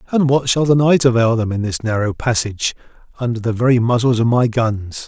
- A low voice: Yes, low, 120 Hz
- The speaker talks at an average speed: No, fast, 215 wpm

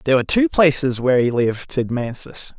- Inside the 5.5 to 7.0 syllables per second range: Yes, 6.1 syllables/s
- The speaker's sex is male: Yes, male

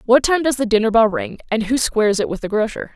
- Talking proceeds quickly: Yes, fast, 285 wpm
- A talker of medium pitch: No, high, 225 Hz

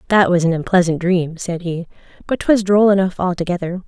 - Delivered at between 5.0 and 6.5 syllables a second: Yes, 5.5 syllables/s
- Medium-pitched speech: Yes, medium, 180 Hz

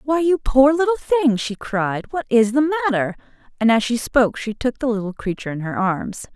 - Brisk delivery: Yes, fast, 215 wpm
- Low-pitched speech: No, high, 245 Hz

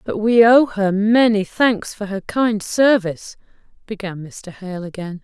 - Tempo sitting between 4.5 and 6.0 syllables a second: No, 4.1 syllables/s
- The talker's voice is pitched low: No, high, 205 Hz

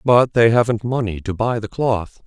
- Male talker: Yes, male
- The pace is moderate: No, fast, 210 wpm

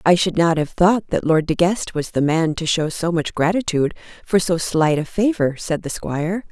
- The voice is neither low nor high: Yes, medium, 170 Hz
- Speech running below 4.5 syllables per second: No, 5.0 syllables/s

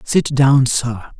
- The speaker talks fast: No, average, 150 wpm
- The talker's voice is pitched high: No, low, 135 Hz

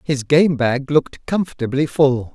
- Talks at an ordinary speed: Yes, average, 155 wpm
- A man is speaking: Yes, male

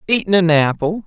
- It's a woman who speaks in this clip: No, male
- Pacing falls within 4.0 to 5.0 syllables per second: Yes, 4.4 syllables/s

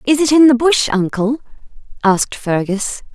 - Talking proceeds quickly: No, average, 155 wpm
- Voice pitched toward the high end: Yes, high, 245 Hz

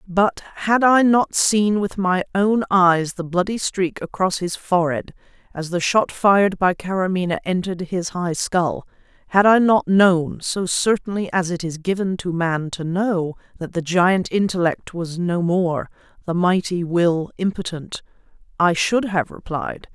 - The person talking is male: No, female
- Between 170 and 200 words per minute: No, average, 160 wpm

